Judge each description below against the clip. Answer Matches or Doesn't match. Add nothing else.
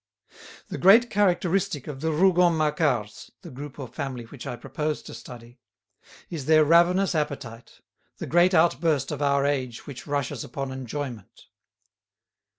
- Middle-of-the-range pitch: Matches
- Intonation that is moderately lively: Matches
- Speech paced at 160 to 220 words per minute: Doesn't match